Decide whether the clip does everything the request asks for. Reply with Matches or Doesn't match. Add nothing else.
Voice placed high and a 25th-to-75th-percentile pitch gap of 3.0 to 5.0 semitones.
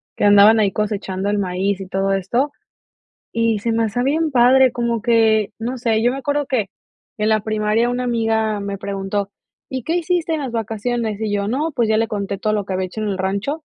Matches